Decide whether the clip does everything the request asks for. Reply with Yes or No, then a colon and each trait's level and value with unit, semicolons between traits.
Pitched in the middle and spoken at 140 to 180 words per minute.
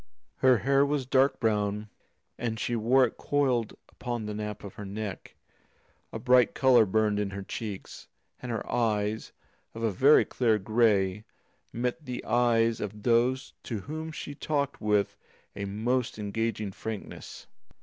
No: low, 115 Hz; average, 150 wpm